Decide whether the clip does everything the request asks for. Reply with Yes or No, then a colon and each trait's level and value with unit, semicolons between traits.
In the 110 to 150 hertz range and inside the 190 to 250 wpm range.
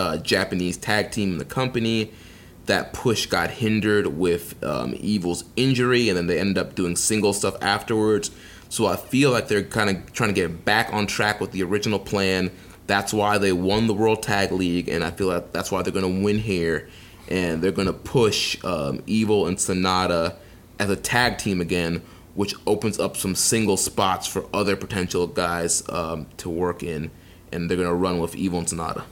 No: very low, 95 Hz; average, 200 wpm